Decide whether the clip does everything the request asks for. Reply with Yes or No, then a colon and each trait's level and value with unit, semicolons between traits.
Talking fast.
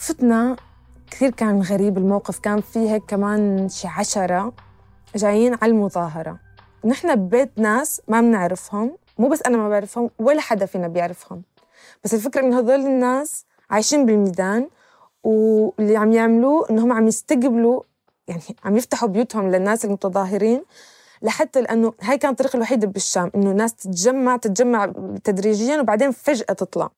Yes: fast, 140 wpm